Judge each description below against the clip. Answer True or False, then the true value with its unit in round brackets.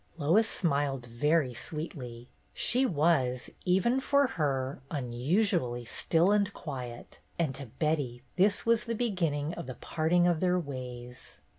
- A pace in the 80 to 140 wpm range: True (135 wpm)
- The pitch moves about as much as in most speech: False (6.1 semitones)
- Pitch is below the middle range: False (155 Hz)